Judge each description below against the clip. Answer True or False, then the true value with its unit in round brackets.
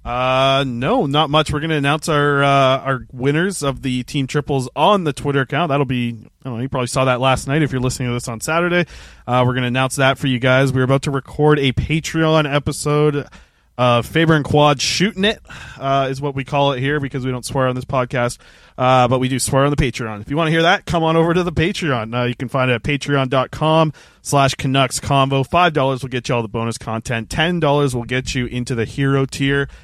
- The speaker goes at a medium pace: False (240 wpm)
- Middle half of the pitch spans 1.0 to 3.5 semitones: True (2.6 semitones)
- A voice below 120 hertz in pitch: False (135 Hz)